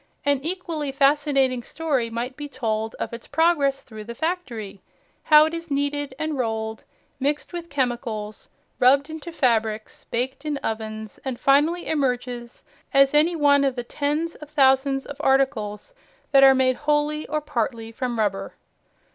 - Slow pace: No, average, 155 wpm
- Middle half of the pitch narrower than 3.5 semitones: No, average, 4.0 semitones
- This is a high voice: Yes, very high, 275 Hz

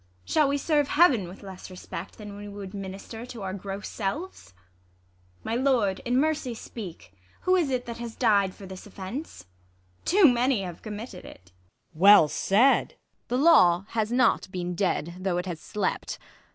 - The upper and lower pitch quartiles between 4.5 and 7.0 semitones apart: Yes, average, 5.0 semitones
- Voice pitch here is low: No, high, 205 Hz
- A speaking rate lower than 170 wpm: No, average, 180 wpm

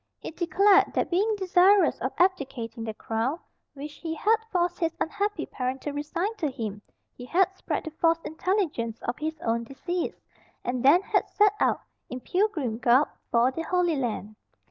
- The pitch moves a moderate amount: No, wide, 6.5 semitones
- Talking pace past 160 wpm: Yes, average, 170 wpm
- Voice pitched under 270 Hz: No, very high, 315 Hz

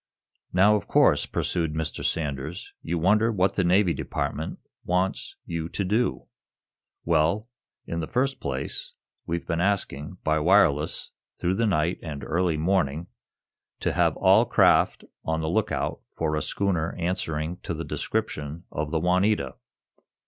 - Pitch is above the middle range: No, very low, 85 Hz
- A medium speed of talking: Yes, average, 145 wpm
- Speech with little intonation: No, average, 3.5 semitones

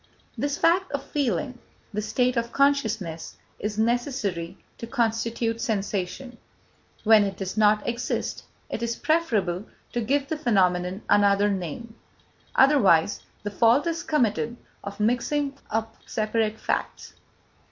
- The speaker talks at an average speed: No, slow, 125 wpm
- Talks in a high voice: Yes, high, 225 Hz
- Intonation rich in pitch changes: No, average, 3.8 semitones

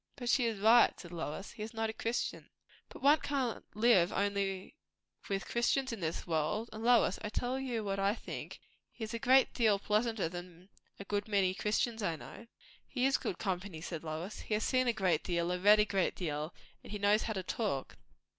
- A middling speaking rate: No, fast, 210 wpm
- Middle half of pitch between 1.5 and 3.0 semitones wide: No, average, 4.0 semitones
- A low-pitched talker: No, high, 205 Hz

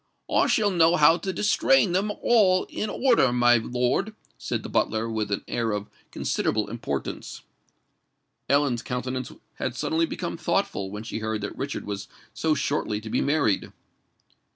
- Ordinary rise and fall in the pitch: No, wide, 7.0 semitones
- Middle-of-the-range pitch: No, low, 125 Hz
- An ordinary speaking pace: Yes, average, 155 wpm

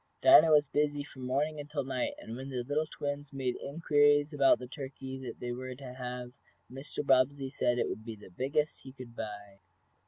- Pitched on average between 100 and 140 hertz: Yes, low, 135 Hz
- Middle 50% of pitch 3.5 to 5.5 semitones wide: No, average, 2.7 semitones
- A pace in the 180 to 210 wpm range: Yes, average, 190 wpm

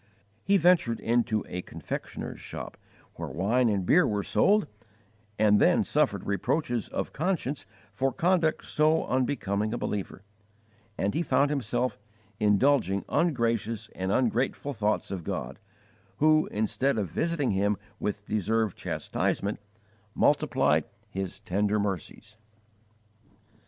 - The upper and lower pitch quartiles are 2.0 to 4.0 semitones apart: No, wide, 5.6 semitones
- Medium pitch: No, low, 110 Hz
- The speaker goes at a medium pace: No, slow, 120 wpm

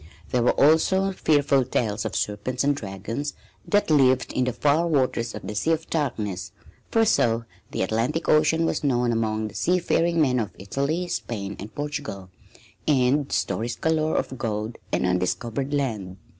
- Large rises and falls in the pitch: Yes, wide, 5.7 semitones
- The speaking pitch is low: Yes, low, 130 Hz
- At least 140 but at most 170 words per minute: Yes, average, 160 wpm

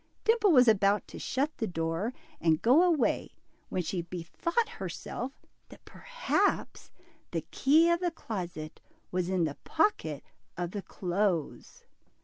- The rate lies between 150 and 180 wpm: No, slow, 135 wpm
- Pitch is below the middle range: No, high, 205 Hz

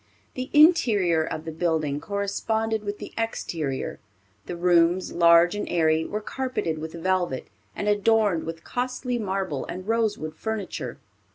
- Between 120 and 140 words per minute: Yes, slow, 135 wpm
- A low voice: No, medium, 185 Hz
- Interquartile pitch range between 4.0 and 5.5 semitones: Yes, average, 5.1 semitones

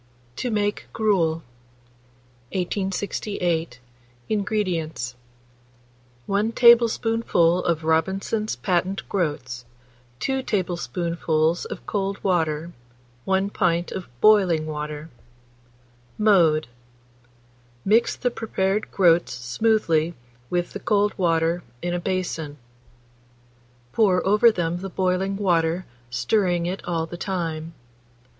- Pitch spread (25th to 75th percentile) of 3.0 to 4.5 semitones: Yes, average, 3.7 semitones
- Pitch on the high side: No, medium, 180 Hz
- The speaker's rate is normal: No, slow, 95 wpm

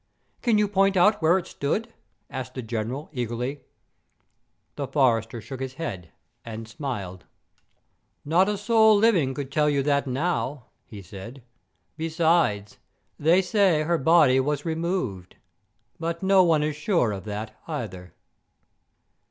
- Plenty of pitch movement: Yes, wide, 6.5 semitones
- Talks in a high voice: No, medium, 145 Hz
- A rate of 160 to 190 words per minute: No, slow, 135 wpm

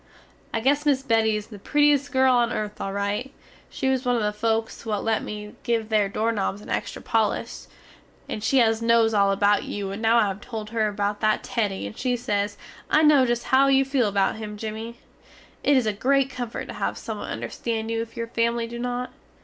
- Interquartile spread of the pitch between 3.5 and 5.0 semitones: No, average, 3.0 semitones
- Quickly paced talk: Yes, fast, 215 wpm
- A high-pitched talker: Yes, high, 225 Hz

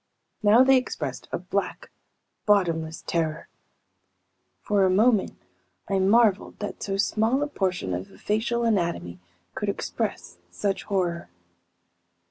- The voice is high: Yes, high, 195 Hz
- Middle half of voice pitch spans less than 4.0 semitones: No, average, 4.5 semitones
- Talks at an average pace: No, slow, 120 wpm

